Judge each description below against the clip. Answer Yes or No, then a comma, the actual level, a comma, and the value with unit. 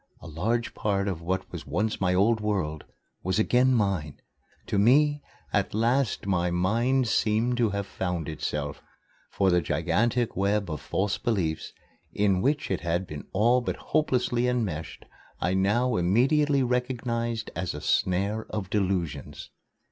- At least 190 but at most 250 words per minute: No, average, 150 wpm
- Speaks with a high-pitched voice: No, low, 105 Hz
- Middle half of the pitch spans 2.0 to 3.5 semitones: No, average, 4.8 semitones